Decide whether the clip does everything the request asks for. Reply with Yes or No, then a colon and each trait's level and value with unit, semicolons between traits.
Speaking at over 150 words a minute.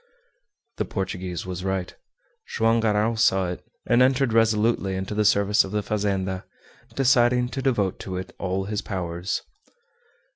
No: average, 145 wpm